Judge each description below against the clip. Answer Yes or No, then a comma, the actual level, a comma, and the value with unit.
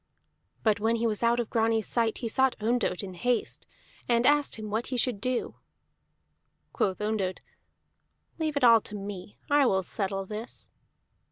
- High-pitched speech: Yes, high, 225 Hz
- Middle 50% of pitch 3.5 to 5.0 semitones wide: No, average, 2.9 semitones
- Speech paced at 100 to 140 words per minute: No, average, 160 wpm